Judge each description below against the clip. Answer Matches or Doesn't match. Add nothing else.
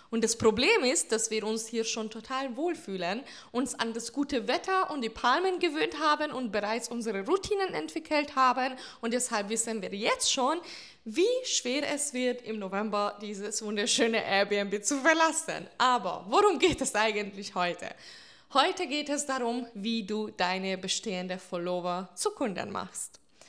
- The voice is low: Doesn't match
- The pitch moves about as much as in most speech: Doesn't match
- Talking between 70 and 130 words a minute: Doesn't match